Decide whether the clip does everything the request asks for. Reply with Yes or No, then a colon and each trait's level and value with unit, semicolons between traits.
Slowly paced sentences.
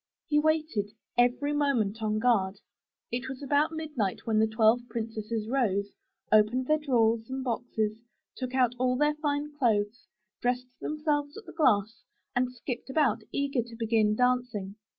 No: average, 155 wpm